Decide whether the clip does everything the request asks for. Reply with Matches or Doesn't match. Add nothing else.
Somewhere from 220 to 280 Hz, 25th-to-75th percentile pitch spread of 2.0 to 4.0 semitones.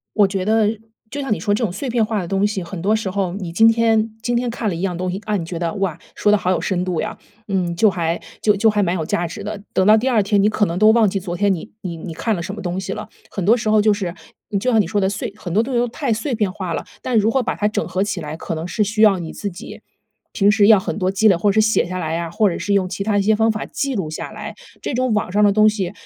Doesn't match